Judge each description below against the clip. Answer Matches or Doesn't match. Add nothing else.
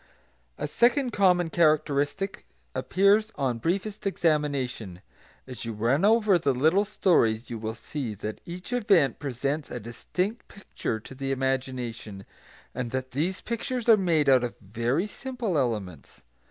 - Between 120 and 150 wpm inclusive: Matches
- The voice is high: Doesn't match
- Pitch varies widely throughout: Matches